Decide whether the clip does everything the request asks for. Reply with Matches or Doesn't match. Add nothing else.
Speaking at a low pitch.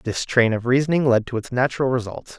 Matches